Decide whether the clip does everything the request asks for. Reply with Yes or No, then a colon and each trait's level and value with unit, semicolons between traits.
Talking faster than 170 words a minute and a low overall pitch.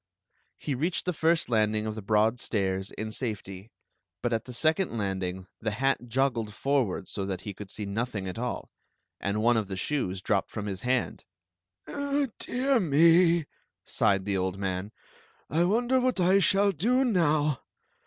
Yes: average, 180 wpm; low, 120 Hz